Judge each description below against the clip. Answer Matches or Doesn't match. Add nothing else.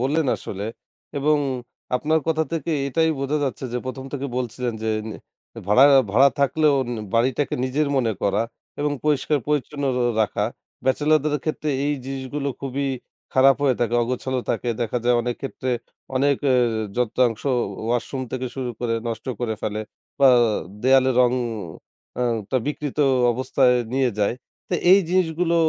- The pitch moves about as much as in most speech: Matches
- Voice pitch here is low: Matches